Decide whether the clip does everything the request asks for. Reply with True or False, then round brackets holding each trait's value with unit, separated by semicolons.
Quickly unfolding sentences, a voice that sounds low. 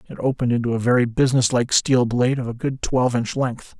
True (220 wpm; 125 Hz)